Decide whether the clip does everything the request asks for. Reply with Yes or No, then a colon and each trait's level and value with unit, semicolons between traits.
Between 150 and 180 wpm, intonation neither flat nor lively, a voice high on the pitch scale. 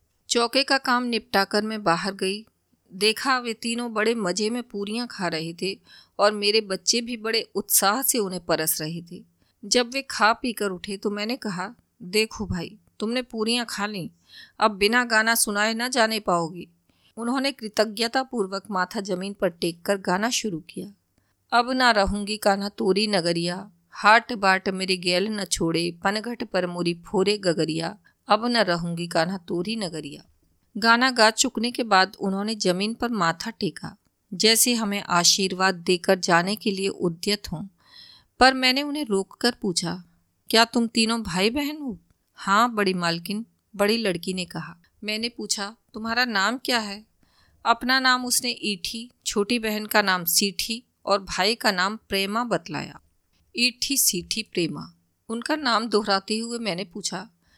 Yes: average, 155 wpm; average, 3.9 semitones; high, 205 Hz